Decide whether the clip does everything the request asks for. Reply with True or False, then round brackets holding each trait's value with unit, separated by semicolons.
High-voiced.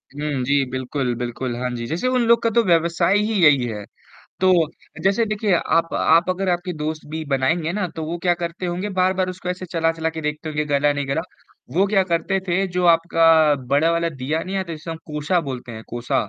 False (165 Hz)